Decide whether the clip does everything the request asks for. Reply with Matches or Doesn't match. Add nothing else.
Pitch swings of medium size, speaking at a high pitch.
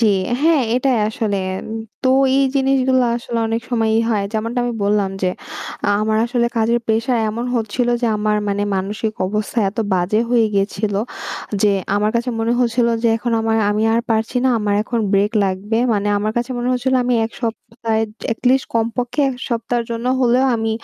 Doesn't match